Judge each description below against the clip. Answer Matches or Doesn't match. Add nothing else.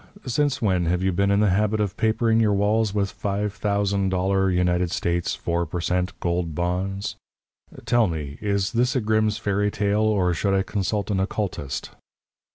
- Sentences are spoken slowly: Doesn't match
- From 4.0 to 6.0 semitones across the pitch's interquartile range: Doesn't match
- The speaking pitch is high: Doesn't match